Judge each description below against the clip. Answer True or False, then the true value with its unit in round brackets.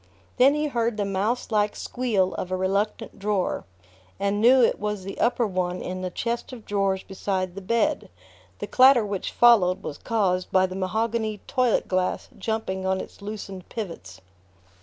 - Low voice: False (200 Hz)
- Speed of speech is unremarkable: True (170 wpm)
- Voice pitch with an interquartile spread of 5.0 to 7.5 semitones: False (3.5 semitones)